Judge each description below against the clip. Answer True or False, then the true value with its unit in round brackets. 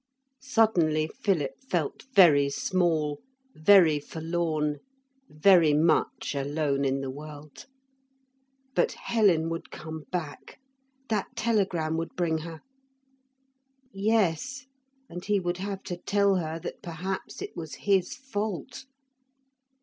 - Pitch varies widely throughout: False (4.2 semitones)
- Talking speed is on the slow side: True (110 wpm)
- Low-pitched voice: False (170 Hz)